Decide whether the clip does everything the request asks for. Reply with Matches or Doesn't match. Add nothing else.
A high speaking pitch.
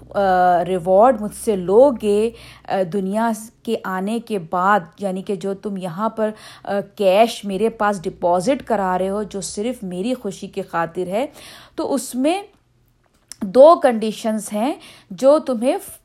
Matches